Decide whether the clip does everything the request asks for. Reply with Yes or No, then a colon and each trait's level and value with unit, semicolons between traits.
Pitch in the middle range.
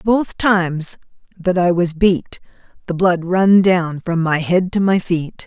Yes: medium, 180 Hz